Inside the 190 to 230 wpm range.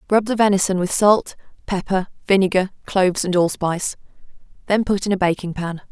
No: average, 160 wpm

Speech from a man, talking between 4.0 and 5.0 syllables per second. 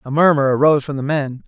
No: male; 6.6 syllables/s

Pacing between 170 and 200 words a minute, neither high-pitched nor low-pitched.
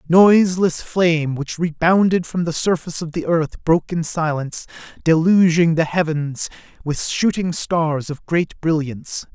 No: average, 140 wpm; medium, 165 Hz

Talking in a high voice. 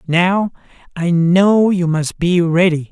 No: medium, 175 Hz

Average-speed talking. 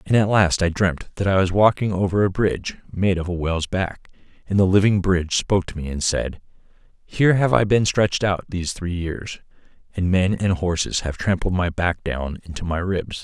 No: fast, 215 wpm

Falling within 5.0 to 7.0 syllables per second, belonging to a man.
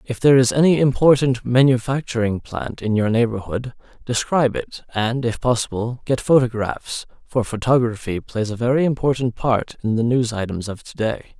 Yes: 5.1 syllables/s; male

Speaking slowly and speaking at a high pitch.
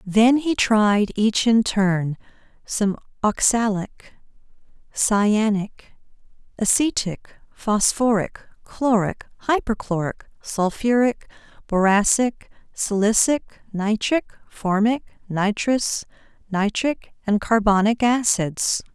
Yes: slow, 75 wpm; high, 215 Hz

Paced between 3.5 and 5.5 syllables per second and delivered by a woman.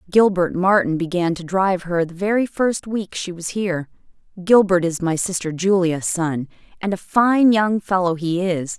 Yes: 4.7 syllables/s; female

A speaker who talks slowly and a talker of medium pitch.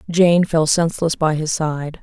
No: average, 180 wpm; medium, 160 Hz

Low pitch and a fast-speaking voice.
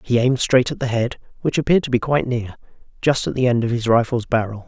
Yes: low, 120 Hz; fast, 245 wpm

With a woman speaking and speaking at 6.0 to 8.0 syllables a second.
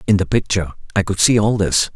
No: male; 6.2 syllables/s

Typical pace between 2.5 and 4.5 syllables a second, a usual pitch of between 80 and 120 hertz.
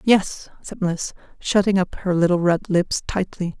No: 4.2 syllables/s; medium, 185 Hz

